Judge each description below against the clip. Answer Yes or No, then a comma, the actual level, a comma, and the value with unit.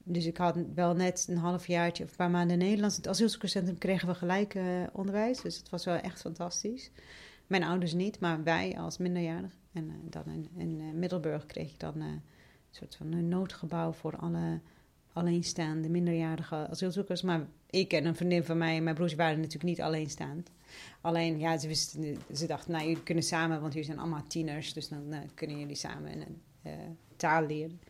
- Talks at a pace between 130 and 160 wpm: No, average, 195 wpm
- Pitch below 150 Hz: No, medium, 170 Hz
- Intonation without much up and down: Yes, narrow, 2.0 semitones